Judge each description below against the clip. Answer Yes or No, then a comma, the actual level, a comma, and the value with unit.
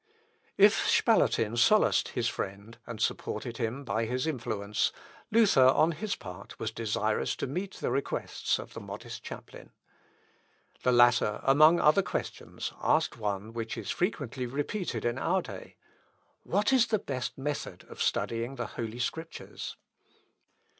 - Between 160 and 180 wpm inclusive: No, average, 140 wpm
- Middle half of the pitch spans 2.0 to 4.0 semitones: No, wide, 5.5 semitones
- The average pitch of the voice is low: Yes, low, 125 Hz